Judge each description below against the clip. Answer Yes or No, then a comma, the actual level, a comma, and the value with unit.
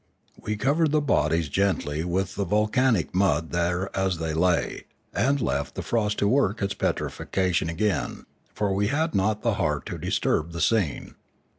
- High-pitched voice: No, very low, 95 Hz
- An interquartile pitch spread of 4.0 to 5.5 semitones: Yes, average, 4.3 semitones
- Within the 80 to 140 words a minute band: No, average, 165 wpm